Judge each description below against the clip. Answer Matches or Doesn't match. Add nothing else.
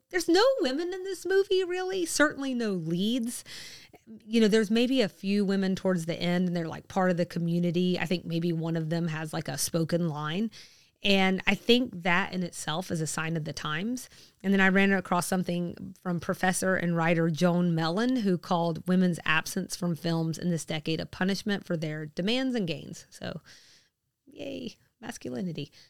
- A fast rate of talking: Doesn't match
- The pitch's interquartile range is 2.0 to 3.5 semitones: Doesn't match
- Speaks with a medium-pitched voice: Matches